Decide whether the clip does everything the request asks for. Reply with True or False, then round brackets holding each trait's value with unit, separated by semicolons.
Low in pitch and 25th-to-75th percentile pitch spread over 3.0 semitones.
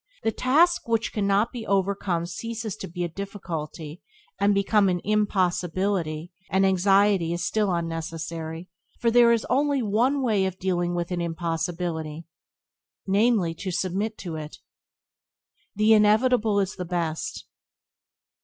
False (190 Hz; 3.8 semitones)